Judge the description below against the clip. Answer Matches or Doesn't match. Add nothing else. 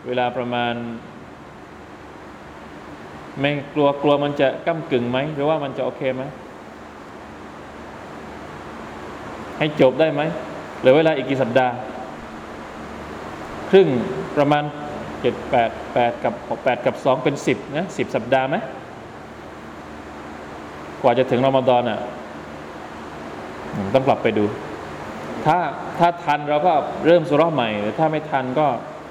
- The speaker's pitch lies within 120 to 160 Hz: Matches